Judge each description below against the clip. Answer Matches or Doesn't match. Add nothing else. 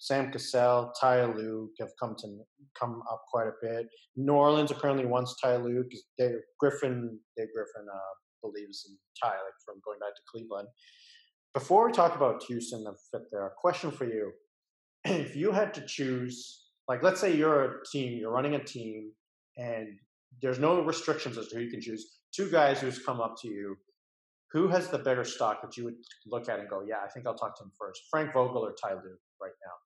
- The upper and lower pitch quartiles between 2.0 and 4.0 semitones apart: Doesn't match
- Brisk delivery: Matches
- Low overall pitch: Matches